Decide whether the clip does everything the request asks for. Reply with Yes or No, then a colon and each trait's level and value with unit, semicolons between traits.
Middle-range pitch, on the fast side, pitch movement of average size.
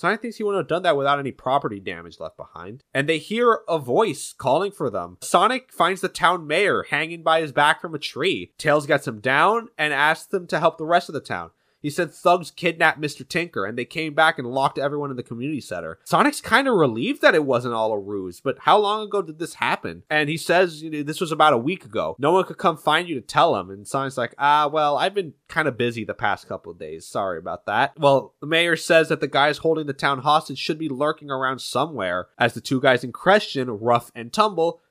Yes: medium, 150 Hz; fast, 250 wpm; average, 4.0 semitones